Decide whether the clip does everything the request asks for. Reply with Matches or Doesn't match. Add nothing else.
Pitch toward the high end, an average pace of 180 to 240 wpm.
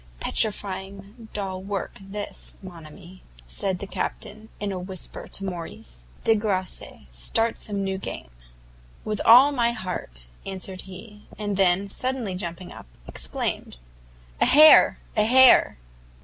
Doesn't match